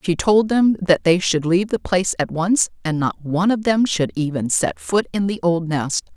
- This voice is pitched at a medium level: Yes, medium, 170 Hz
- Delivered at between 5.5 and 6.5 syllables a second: No, 5.0 syllables/s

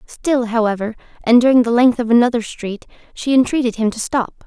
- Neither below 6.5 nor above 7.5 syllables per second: No, 5.5 syllables/s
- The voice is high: Yes, high, 235 Hz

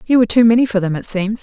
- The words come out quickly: Yes, fast, 335 wpm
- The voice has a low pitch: No, high, 215 Hz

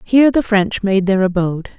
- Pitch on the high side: Yes, high, 205 Hz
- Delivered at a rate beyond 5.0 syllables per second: Yes, 5.6 syllables/s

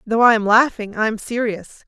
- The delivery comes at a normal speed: No, fast, 225 wpm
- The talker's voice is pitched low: No, high, 220 Hz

